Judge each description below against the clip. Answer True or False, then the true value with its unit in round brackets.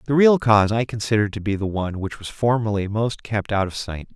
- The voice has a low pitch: True (110 Hz)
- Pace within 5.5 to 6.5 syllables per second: True (5.8 syllables/s)